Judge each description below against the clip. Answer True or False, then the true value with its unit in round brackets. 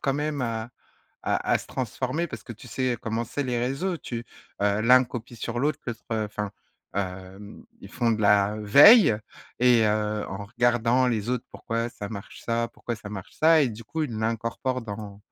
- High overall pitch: False (115 Hz)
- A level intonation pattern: False (3.1 semitones)